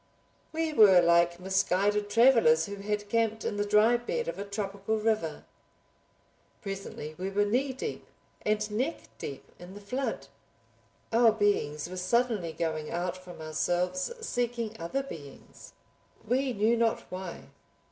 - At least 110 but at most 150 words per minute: Yes, slow, 135 wpm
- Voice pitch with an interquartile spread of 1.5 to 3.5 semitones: No, average, 4.2 semitones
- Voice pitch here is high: Yes, high, 205 Hz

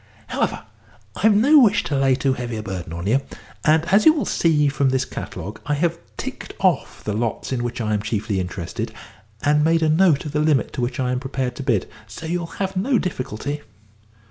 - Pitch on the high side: No, medium, 140 Hz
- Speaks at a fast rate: Yes, fast, 215 wpm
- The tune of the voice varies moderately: No, wide, 5.7 semitones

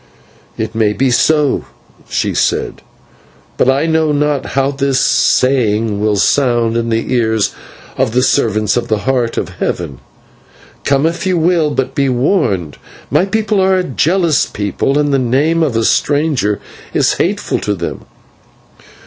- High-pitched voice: No, low, 135 Hz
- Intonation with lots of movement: No, average, 5.0 semitones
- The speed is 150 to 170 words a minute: Yes, average, 155 wpm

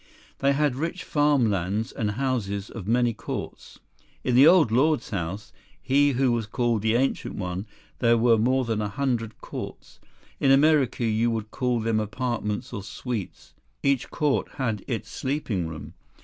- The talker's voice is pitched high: No, low, 120 Hz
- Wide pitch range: No, average, 3.9 semitones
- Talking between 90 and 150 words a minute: No, average, 165 wpm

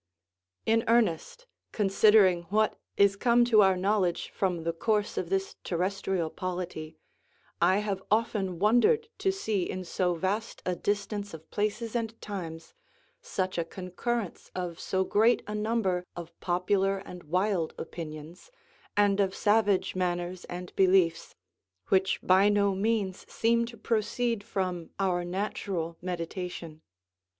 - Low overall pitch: No, high, 190 Hz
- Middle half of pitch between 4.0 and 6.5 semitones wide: No, average, 3.0 semitones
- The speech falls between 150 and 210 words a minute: No, slow, 135 wpm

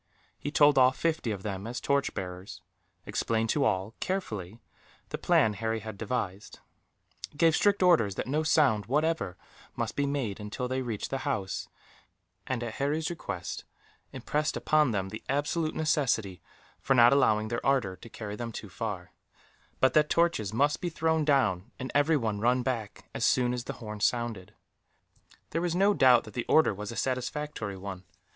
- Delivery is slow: No, average, 170 wpm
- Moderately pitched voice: No, low, 125 Hz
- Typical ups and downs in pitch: No, wide, 5.8 semitones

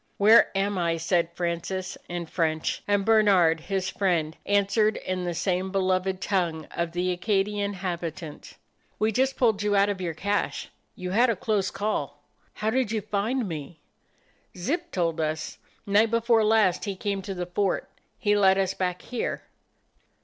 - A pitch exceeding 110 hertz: Yes, high, 190 Hz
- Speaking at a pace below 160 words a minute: No, average, 165 wpm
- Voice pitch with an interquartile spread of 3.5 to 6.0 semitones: No, average, 3.0 semitones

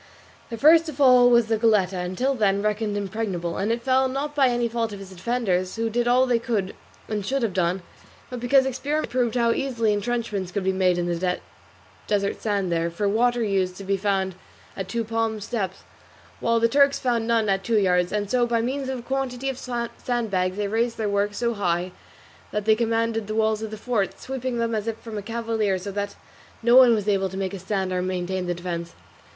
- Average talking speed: No, fast, 220 wpm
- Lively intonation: No, average, 3.8 semitones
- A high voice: Yes, high, 220 Hz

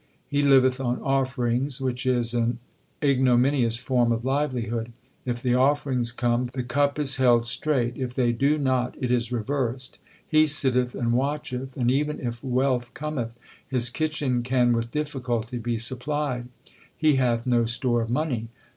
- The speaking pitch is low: Yes, low, 125 Hz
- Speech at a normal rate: Yes, average, 155 wpm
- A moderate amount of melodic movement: No, narrow, 2.2 semitones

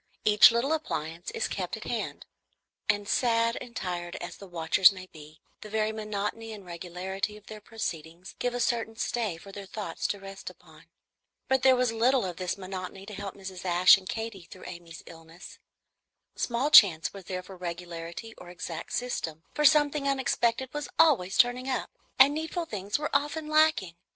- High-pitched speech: Yes, high, 205 Hz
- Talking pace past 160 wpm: Yes, average, 180 wpm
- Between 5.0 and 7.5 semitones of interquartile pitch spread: Yes, average, 5.3 semitones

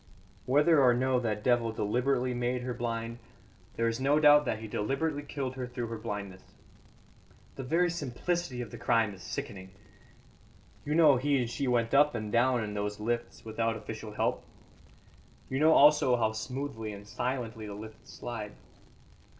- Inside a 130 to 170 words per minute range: Yes, average, 165 wpm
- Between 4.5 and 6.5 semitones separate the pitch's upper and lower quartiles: No, average, 3.5 semitones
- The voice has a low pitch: Yes, low, 120 Hz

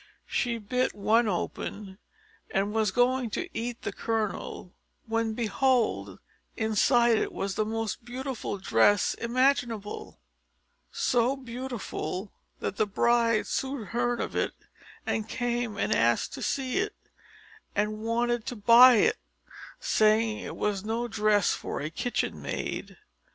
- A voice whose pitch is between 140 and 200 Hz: No, high, 225 Hz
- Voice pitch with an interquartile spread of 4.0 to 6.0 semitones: No, narrow, 2.6 semitones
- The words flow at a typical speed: No, slow, 130 wpm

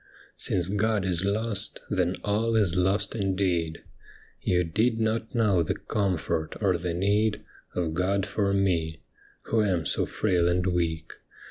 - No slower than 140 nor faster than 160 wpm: Yes, average, 150 wpm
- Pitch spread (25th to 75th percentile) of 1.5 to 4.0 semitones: Yes, average, 3.1 semitones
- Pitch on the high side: No, very low, 95 Hz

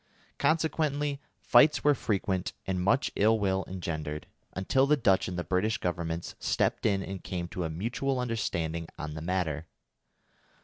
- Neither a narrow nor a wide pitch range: No, wide, 6.0 semitones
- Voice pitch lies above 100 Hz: No, very low, 95 Hz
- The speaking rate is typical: Yes, average, 150 wpm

